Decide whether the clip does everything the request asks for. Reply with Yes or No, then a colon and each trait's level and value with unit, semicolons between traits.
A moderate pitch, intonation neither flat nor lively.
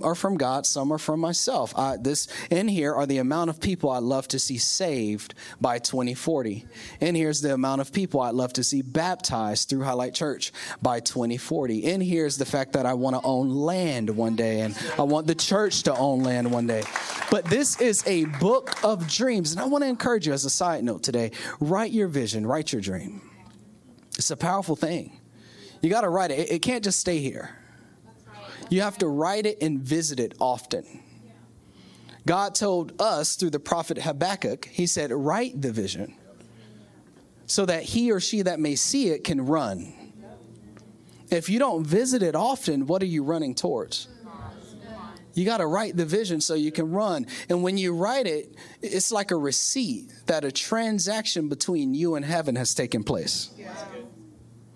No: medium, 155 Hz; wide, 6.6 semitones